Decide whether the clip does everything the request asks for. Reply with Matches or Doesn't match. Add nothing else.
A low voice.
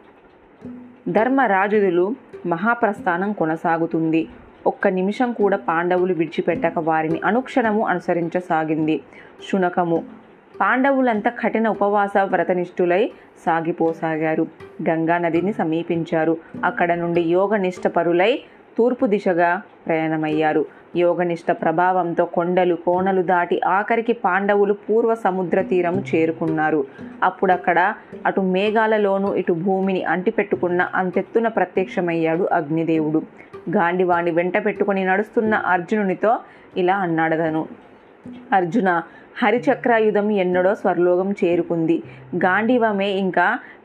Doesn't match